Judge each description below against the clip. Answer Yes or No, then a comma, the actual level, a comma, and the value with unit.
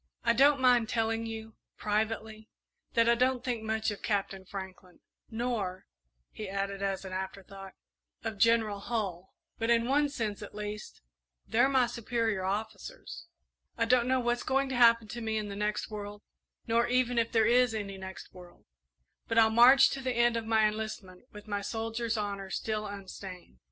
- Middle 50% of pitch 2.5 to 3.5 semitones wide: Yes, average, 2.8 semitones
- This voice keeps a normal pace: Yes, average, 175 wpm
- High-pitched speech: Yes, high, 220 Hz